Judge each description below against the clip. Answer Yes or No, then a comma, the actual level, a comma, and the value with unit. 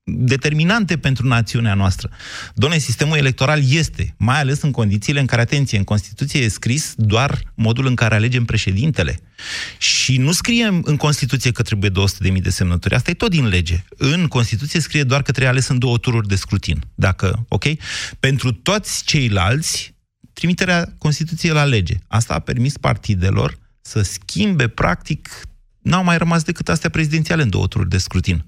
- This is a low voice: Yes, low, 125 Hz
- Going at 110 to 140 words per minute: No, fast, 170 wpm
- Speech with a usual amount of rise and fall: No, wide, 6.2 semitones